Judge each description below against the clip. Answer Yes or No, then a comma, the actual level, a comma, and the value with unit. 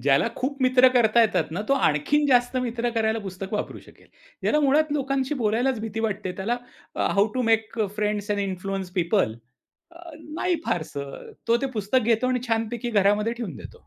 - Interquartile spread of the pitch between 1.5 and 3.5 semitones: No, average, 4.0 semitones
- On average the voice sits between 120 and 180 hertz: No, high, 225 Hz